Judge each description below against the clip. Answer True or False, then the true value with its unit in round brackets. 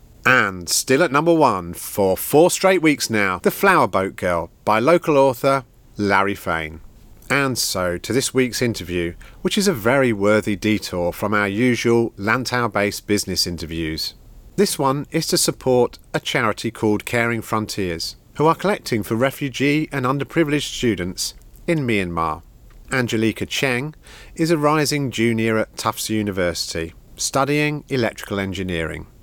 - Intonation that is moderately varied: False (5.8 semitones)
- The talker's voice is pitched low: True (115 Hz)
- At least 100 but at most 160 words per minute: True (140 wpm)